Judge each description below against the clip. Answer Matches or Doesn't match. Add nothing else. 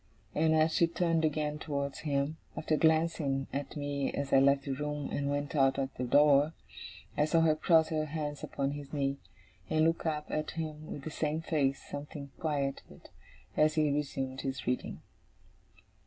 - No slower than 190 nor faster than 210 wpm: Doesn't match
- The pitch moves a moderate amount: Doesn't match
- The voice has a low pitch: Doesn't match